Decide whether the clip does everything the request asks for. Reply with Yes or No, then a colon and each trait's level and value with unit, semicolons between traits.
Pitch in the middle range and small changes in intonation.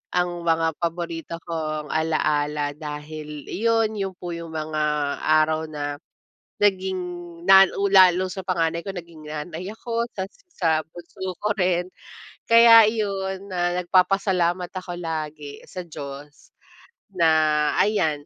No: medium, 175 Hz; average, 3.5 semitones